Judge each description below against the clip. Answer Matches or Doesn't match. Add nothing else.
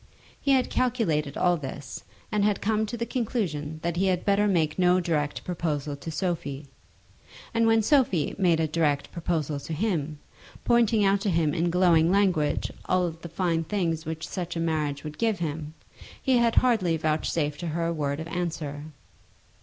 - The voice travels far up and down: Doesn't match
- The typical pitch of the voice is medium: Matches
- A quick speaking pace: Doesn't match